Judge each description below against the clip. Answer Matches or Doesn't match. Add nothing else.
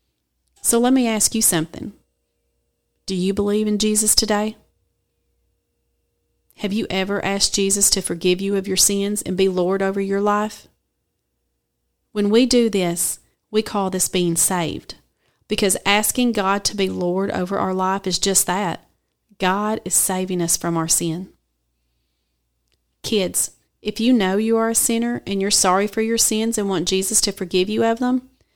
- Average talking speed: Matches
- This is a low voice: Doesn't match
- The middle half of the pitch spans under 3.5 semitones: Matches